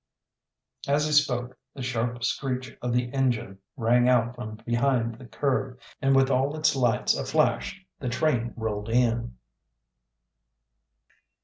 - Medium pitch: No, low, 125 Hz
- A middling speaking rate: No, slow, 130 wpm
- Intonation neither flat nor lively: No, narrow, 2.2 semitones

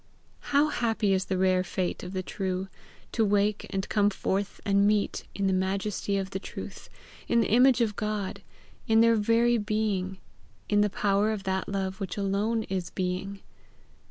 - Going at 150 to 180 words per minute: Yes, average, 170 wpm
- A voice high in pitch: Yes, high, 200 Hz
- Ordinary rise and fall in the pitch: No, narrow, 2.0 semitones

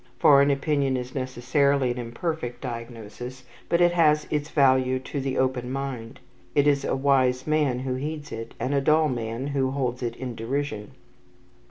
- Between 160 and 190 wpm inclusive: Yes, average, 170 wpm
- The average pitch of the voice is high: No, low, 130 Hz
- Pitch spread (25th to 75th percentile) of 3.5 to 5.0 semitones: No, narrow, 2.4 semitones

